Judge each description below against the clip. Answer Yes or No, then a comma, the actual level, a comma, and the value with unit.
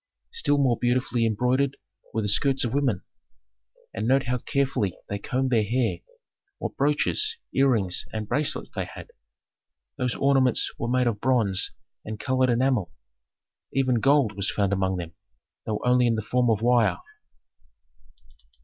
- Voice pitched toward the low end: Yes, low, 125 Hz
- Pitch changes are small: No, average, 3.6 semitones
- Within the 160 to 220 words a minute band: No, average, 150 wpm